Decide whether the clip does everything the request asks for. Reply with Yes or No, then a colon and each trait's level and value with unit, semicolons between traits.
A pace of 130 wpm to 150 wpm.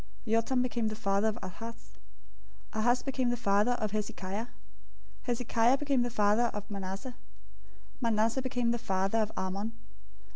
Yes: average, 145 wpm